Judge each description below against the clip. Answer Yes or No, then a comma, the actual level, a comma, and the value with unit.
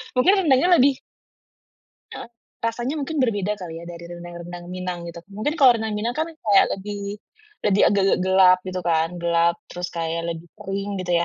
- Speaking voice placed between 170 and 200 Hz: Yes, high, 190 Hz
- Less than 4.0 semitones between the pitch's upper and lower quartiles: No, average, 4.6 semitones